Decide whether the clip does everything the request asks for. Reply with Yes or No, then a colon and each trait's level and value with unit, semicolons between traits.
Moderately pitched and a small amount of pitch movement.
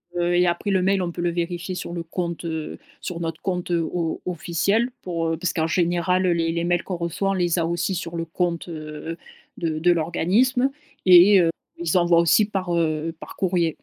Yes: medium, 175 Hz; narrow, 1.5 semitones